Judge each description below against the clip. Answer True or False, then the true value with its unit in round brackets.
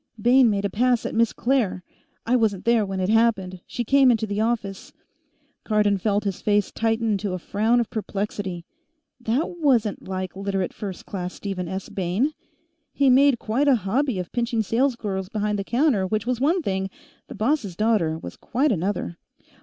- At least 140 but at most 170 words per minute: False (180 wpm)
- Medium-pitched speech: False (215 Hz)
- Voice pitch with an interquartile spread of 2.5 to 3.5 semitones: False (3.9 semitones)